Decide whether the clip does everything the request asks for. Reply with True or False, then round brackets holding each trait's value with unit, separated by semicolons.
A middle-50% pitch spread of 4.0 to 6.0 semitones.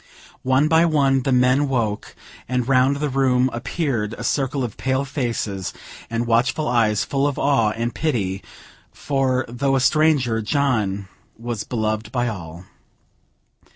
False (3.3 semitones)